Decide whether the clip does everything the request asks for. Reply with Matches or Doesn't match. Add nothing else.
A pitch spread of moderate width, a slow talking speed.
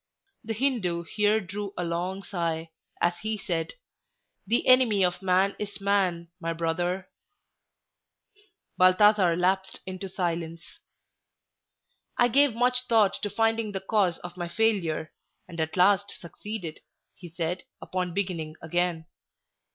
Matches